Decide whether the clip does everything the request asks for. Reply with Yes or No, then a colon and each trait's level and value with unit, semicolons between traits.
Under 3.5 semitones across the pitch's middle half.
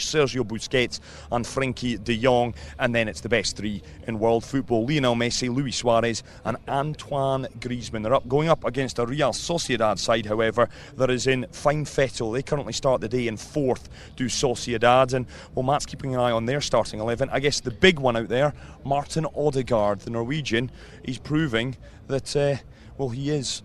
Yes: average, 3.1 semitones